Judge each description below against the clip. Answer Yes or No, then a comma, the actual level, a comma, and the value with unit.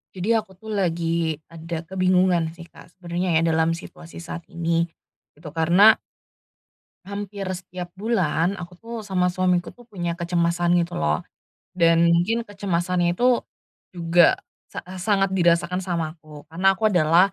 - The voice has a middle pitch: Yes, medium, 175 Hz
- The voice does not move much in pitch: Yes, narrow, 2.1 semitones